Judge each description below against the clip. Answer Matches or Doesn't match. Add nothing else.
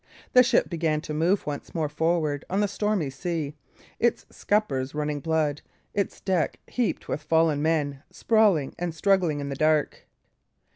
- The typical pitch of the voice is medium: Matches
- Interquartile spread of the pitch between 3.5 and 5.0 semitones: Matches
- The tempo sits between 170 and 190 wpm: Doesn't match